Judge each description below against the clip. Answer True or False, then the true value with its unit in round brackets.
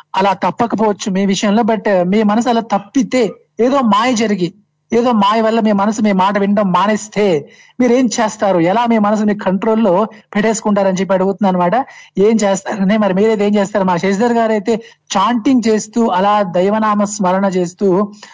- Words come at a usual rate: False (165 wpm)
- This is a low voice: False (210 Hz)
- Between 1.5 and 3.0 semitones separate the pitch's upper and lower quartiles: True (2.4 semitones)